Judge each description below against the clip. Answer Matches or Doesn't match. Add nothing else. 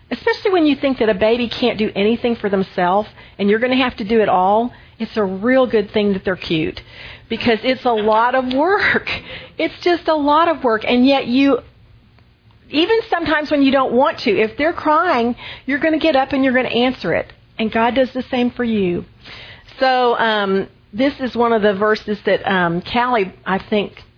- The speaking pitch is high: Matches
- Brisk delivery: Matches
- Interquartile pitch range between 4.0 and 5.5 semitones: Matches